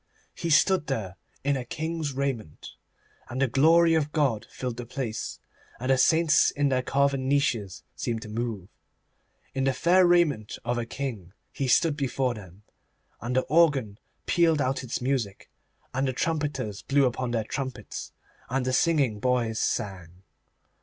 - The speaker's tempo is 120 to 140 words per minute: No, average, 160 wpm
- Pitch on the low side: Yes, low, 130 Hz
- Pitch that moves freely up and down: No, average, 3.9 semitones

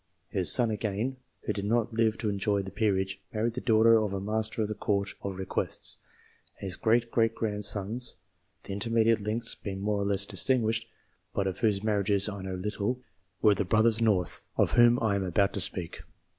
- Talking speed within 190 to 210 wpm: Yes, average, 200 wpm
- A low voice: Yes, low, 105 Hz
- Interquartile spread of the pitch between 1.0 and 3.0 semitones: Yes, narrow, 2.4 semitones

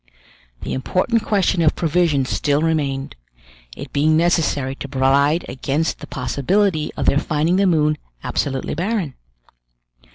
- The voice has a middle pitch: Yes, medium, 155 Hz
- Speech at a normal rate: No, slow, 130 wpm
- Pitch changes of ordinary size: Yes, average, 3.8 semitones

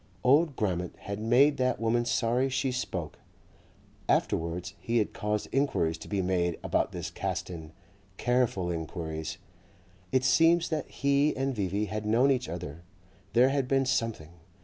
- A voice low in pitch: Yes, low, 115 Hz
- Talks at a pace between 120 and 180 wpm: Yes, average, 150 wpm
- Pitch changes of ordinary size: No, wide, 6.6 semitones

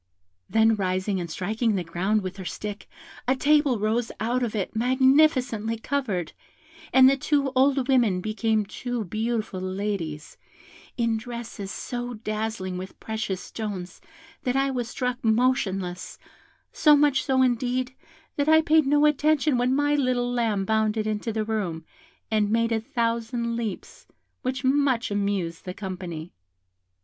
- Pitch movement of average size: Yes, average, 4.2 semitones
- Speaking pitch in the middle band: No, high, 225 Hz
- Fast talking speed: No, average, 145 wpm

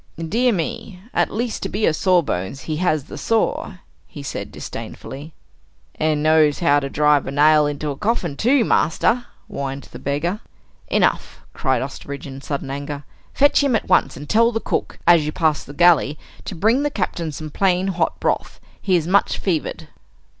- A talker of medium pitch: Yes, medium, 160 Hz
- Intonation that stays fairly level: No, wide, 5.4 semitones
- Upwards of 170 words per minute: Yes, average, 180 wpm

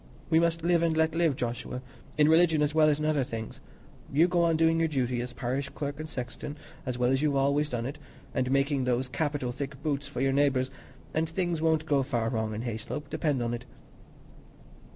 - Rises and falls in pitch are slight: No, average, 3.8 semitones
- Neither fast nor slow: No, fast, 215 wpm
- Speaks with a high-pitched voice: No, medium, 145 Hz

